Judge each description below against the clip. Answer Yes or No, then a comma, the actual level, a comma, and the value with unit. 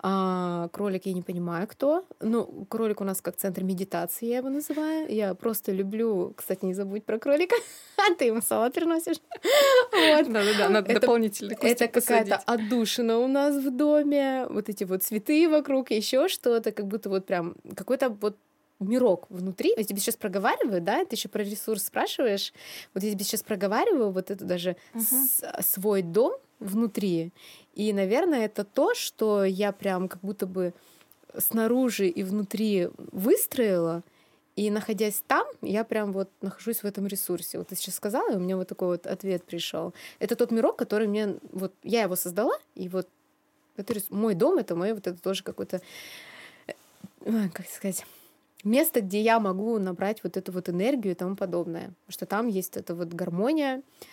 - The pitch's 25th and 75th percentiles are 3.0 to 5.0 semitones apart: Yes, average, 3.8 semitones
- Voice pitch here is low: No, high, 210 Hz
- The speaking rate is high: Yes, fast, 165 wpm